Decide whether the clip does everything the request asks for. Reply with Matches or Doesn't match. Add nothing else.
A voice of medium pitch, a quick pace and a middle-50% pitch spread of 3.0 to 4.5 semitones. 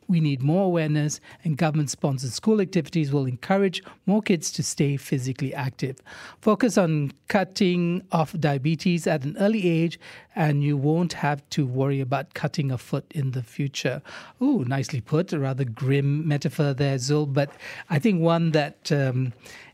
Doesn't match